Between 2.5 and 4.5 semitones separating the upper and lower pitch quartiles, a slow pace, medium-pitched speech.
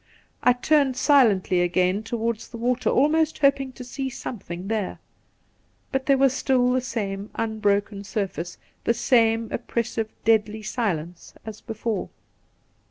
No: average, 3.9 semitones; slow, 130 wpm; high, 225 Hz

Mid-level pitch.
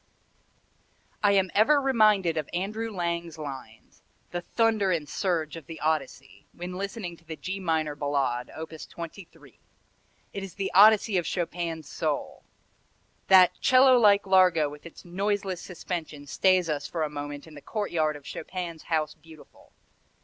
Yes: medium, 170 Hz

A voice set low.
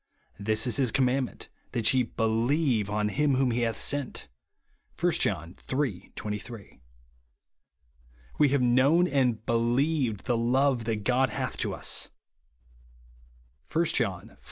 Yes: low, 120 Hz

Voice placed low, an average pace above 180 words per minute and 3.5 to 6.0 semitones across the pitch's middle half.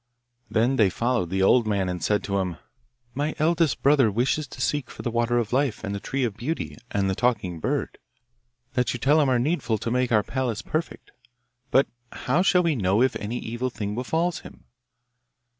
Yes: low, 120 Hz; average, 200 wpm; average, 4.7 semitones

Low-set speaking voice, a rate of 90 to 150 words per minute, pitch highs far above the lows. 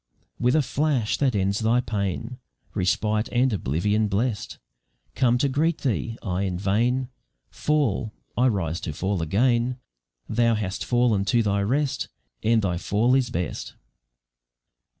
No: low, 110 Hz; average, 140 wpm; average, 4.0 semitones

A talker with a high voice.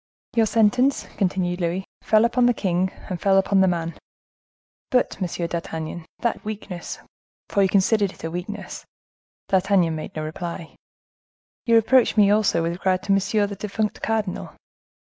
Yes: high, 195 Hz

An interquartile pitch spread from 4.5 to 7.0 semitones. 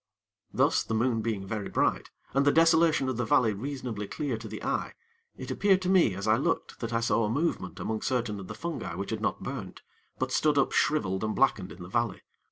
Yes: average, 5.1 semitones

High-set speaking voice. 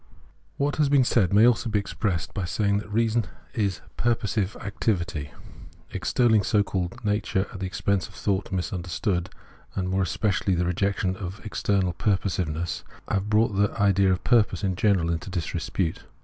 No: low, 100 Hz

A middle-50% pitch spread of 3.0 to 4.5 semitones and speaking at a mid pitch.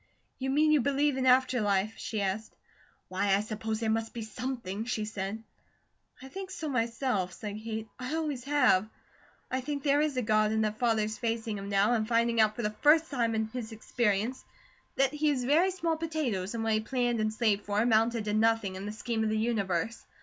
No: average, 3.4 semitones; high, 225 Hz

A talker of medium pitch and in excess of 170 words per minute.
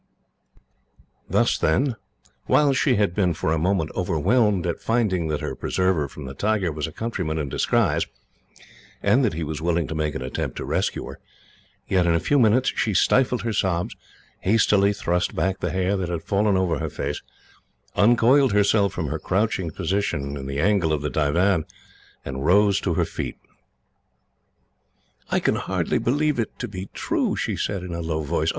No: very low, 95 Hz; average, 180 wpm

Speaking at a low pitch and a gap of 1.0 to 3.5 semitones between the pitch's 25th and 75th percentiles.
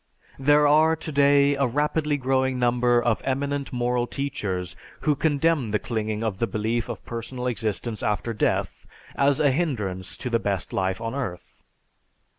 No: low, 125 Hz; average, 4.4 semitones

